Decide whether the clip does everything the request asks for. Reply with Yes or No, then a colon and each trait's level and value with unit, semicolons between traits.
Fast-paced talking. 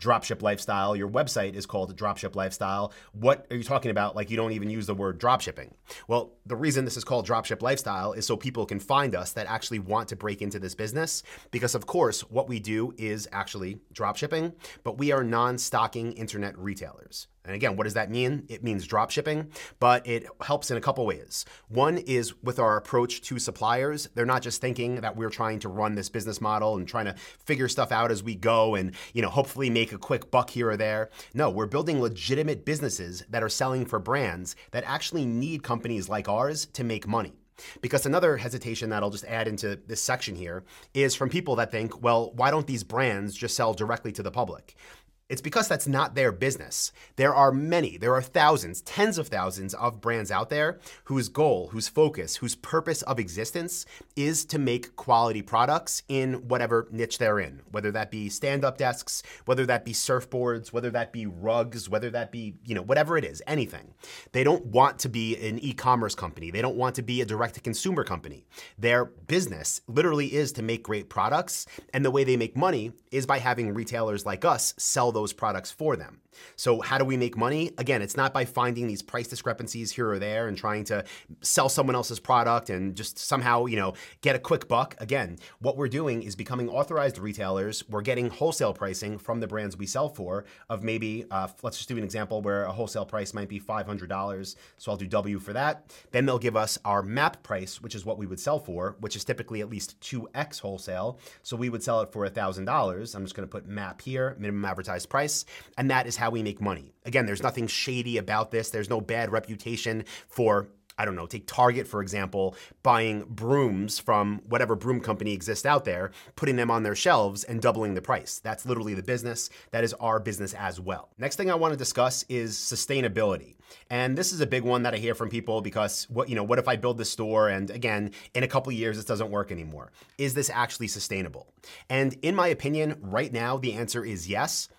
Yes: fast, 215 wpm